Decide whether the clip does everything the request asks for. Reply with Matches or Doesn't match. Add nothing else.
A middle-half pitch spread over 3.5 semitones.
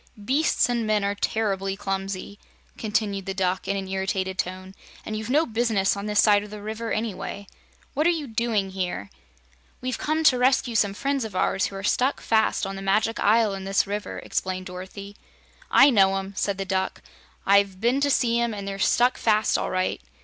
Doesn't match